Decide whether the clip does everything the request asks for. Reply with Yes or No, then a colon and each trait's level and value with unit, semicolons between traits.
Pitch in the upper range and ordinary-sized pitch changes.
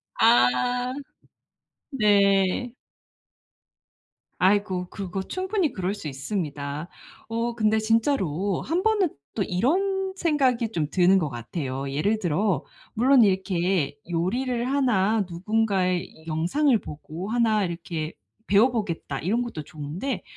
No: high, 200 Hz; wide, 6.1 semitones